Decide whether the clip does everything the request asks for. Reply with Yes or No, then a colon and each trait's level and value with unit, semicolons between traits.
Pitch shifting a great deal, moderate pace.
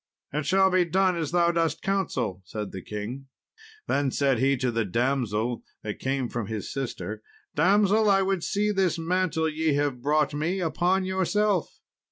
Yes: wide, 6.9 semitones; average, 170 wpm